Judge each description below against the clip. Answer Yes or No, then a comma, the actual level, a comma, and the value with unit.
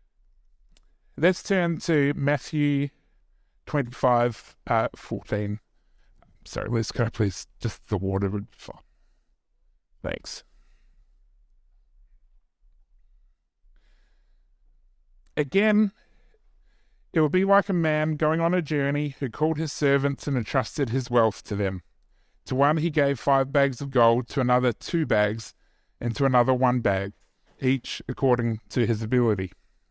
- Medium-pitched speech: No, low, 125 Hz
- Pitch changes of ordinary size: No, wide, 6.1 semitones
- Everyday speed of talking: No, slow, 120 wpm